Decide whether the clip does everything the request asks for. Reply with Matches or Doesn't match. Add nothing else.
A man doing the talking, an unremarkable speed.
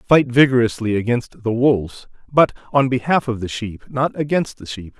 Matches